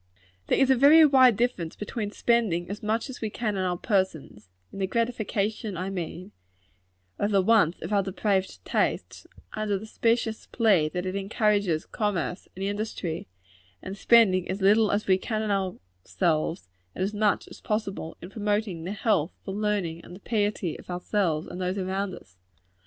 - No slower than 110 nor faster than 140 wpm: No, average, 175 wpm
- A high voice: Yes, high, 200 Hz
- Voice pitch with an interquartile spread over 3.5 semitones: No, average, 2.8 semitones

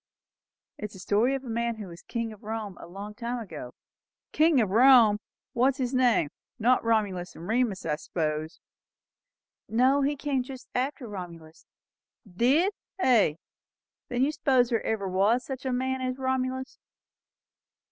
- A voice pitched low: No, high, 235 Hz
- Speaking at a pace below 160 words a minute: No, average, 165 wpm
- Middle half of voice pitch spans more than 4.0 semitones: Yes, average, 4.6 semitones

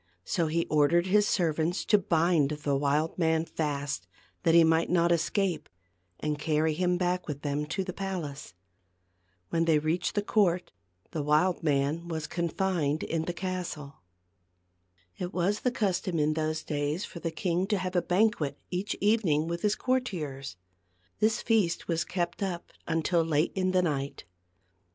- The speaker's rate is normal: Yes, average, 170 wpm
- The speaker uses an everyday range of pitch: Yes, average, 3.3 semitones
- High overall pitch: No, medium, 170 Hz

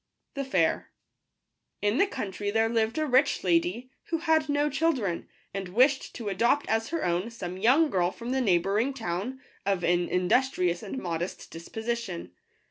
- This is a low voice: No, high, 225 Hz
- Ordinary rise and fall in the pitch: No, wide, 6.6 semitones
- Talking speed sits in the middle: Yes, average, 175 wpm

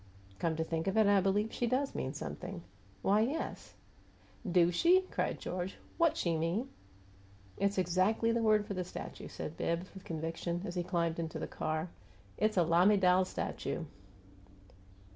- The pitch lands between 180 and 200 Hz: Yes, medium, 185 Hz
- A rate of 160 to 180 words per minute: Yes, average, 165 wpm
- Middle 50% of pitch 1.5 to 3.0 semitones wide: No, average, 4.0 semitones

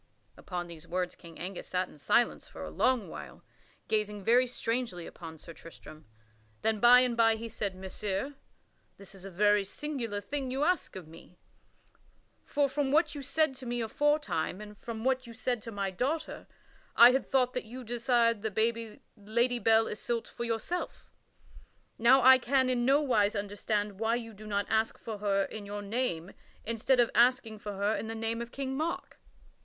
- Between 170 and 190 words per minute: Yes, average, 185 wpm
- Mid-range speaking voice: No, high, 225 Hz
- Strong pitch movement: No, average, 3.7 semitones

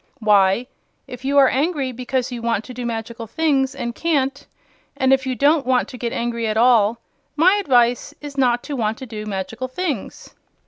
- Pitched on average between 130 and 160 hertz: No, very high, 250 Hz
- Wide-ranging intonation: No, average, 2.9 semitones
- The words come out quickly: No, average, 190 wpm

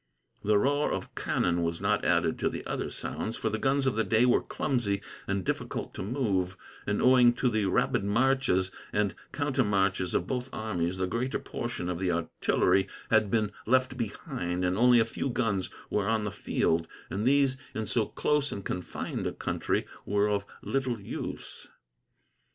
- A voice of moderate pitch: No, low, 105 Hz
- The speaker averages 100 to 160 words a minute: No, average, 175 wpm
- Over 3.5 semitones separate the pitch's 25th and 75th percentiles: Yes, average, 4.6 semitones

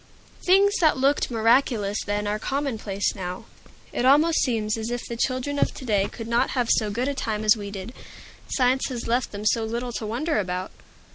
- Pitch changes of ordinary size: Yes, average, 3.8 semitones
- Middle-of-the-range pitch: No, high, 235 Hz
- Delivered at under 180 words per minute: No, average, 200 wpm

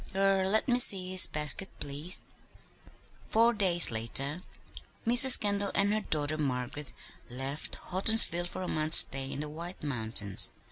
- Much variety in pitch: Yes, wide, 5.8 semitones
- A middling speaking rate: Yes, average, 145 wpm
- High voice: No, medium, 170 Hz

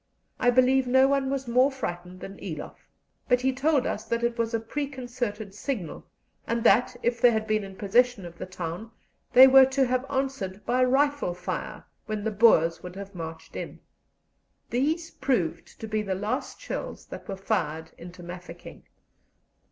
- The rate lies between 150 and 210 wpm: Yes, average, 175 wpm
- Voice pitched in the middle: No, high, 230 Hz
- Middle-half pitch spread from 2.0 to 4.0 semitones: No, wide, 5.5 semitones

